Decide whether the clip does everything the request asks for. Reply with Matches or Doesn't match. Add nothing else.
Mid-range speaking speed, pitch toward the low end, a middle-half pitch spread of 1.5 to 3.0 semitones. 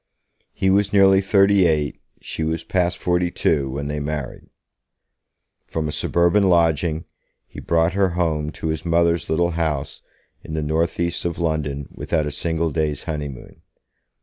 Matches